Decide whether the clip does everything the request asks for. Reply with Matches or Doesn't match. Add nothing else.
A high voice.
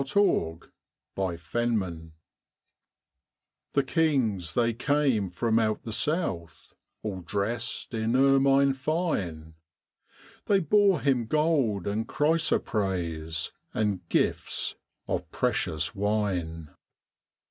Doesn't match